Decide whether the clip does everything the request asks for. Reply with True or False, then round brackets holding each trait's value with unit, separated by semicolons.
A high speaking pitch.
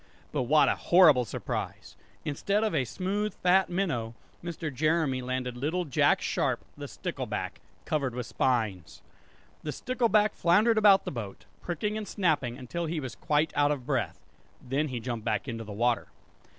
False (150 Hz)